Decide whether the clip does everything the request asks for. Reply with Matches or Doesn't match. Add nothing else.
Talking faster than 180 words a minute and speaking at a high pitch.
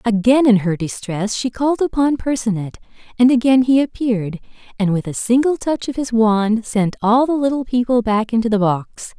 Matches